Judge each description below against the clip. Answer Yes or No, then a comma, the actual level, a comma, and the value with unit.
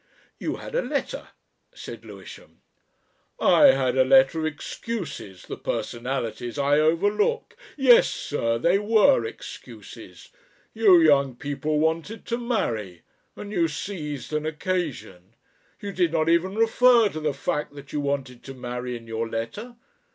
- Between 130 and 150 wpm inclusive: Yes, average, 145 wpm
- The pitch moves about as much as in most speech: No, wide, 7.6 semitones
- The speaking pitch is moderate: Yes, medium, 155 Hz